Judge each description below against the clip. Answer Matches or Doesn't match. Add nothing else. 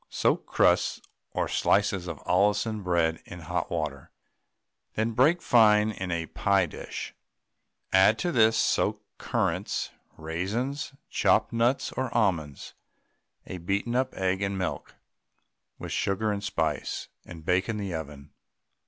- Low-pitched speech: Matches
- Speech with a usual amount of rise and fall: Matches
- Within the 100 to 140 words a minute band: Matches